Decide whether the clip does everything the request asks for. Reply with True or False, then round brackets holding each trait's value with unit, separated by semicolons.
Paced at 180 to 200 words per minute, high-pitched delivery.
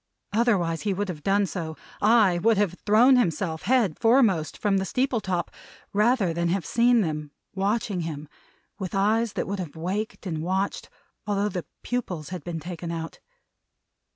False (165 wpm; 195 Hz)